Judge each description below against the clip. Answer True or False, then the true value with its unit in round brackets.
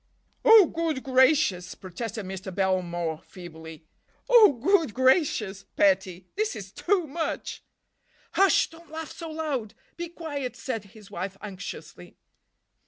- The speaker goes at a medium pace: False (110 wpm)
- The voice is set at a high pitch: True (235 Hz)